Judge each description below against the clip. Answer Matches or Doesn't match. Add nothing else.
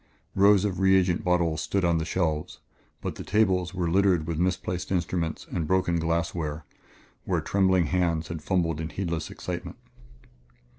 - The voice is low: Matches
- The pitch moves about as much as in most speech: Doesn't match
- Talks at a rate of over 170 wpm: Doesn't match